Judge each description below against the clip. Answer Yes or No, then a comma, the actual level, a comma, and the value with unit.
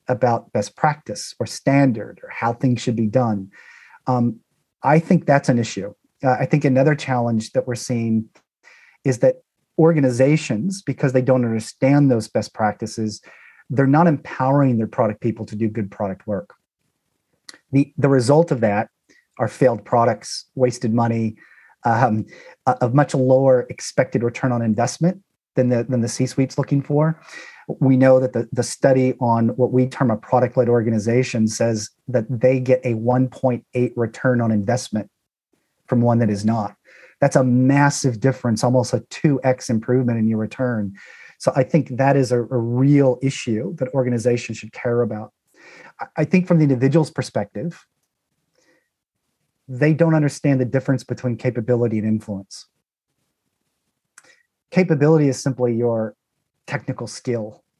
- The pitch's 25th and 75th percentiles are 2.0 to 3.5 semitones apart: Yes, average, 3.0 semitones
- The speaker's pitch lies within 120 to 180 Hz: Yes, low, 125 Hz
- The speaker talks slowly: No, average, 155 wpm